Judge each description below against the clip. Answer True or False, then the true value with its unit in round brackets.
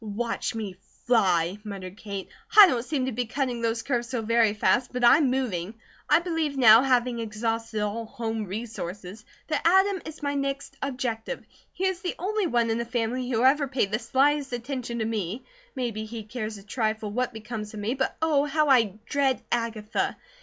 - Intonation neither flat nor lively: True (3.8 semitones)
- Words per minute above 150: True (190 wpm)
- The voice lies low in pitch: False (235 Hz)